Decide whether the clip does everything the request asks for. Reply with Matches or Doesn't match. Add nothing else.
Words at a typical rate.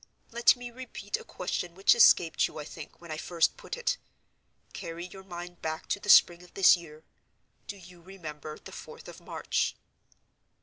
Matches